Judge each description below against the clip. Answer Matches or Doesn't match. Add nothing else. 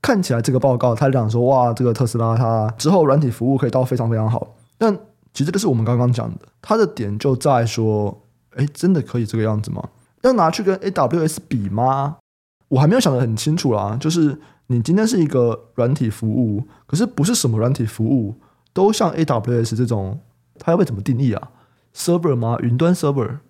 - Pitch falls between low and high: Doesn't match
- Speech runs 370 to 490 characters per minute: Doesn't match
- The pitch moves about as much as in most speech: Matches